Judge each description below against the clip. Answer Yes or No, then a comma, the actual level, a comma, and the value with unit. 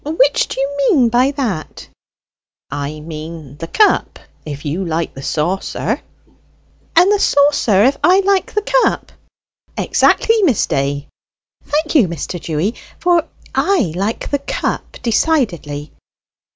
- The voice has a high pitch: Yes, high, 230 Hz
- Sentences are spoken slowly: Yes, slow, 130 wpm